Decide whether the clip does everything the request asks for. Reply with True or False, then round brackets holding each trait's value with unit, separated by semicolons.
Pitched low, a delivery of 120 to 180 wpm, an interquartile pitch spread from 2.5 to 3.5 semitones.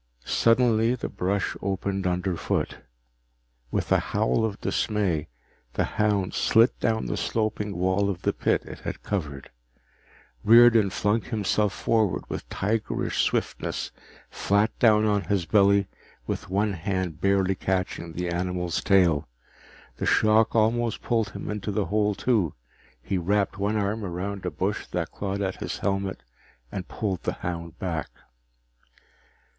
True (100 Hz; 140 wpm; 2.8 semitones)